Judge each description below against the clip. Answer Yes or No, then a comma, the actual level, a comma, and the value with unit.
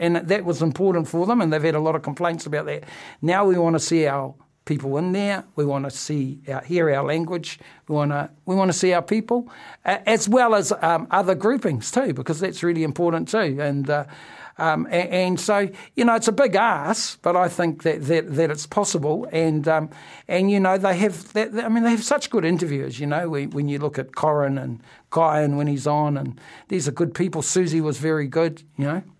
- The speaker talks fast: Yes, fast, 235 wpm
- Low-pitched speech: No, medium, 165 Hz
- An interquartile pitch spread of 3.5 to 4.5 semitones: Yes, average, 4.2 semitones